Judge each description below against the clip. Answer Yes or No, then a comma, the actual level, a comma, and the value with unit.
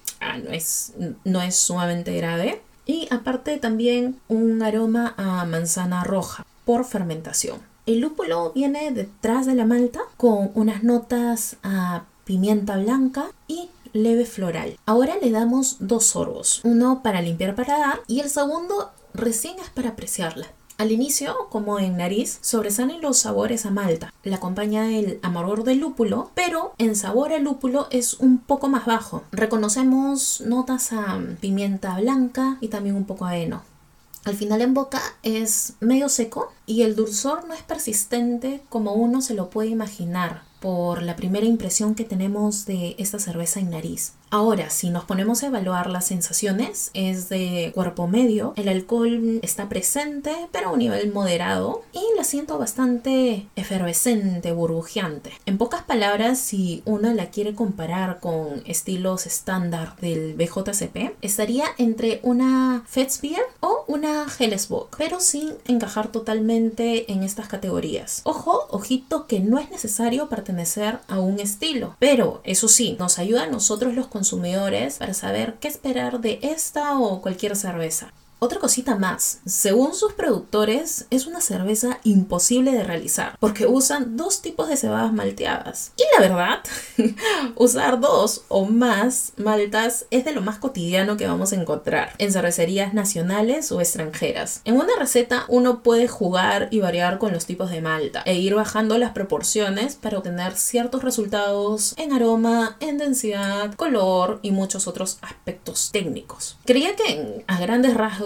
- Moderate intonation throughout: Yes, average, 4.5 semitones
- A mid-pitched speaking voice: No, high, 225 Hz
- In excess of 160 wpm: No, average, 155 wpm